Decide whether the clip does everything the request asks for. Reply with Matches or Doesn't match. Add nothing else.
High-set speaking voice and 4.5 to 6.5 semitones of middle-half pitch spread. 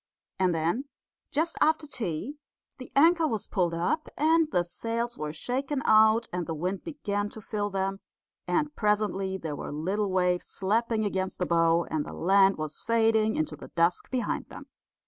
Matches